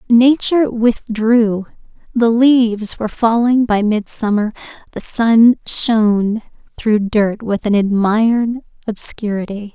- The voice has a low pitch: No, high, 225 Hz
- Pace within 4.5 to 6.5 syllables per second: No, 3.9 syllables/s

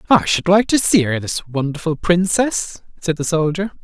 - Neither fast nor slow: Yes, average, 190 wpm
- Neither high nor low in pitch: Yes, medium, 175 Hz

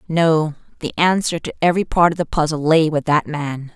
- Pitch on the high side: No, medium, 160 Hz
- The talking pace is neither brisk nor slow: No, fast, 210 wpm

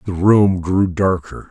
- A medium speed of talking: Yes, average, 160 wpm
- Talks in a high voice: No, very low, 95 Hz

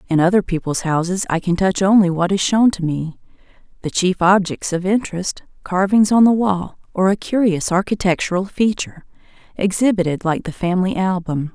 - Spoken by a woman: Yes, female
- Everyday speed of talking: Yes, average, 160 wpm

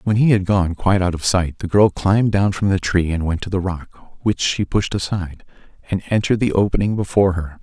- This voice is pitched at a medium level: No, very low, 95 Hz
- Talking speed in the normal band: No, fast, 235 wpm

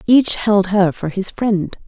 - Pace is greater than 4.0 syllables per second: No, 3.6 syllables/s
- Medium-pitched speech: No, high, 195 Hz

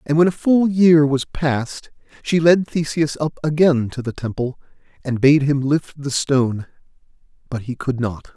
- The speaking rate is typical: Yes, average, 180 wpm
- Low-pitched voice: No, medium, 145 Hz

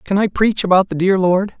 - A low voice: No, high, 190 Hz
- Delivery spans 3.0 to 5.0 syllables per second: No, 5.4 syllables/s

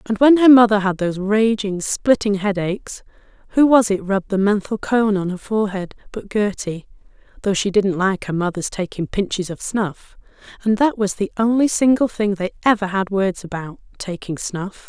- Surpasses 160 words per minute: Yes, average, 180 wpm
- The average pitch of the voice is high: Yes, high, 205 Hz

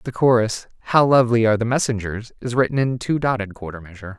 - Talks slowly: No, average, 200 wpm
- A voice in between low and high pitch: No, low, 115 Hz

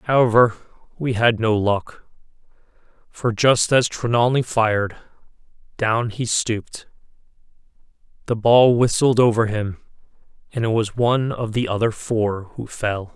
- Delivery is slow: Yes, slow, 130 wpm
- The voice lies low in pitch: Yes, low, 115 Hz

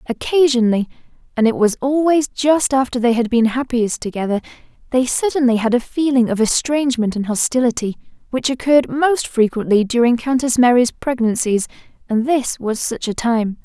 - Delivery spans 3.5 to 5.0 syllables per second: No, 5.3 syllables/s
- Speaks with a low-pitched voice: No, high, 245 Hz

